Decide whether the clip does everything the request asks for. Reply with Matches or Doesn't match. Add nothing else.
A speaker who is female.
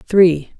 Matches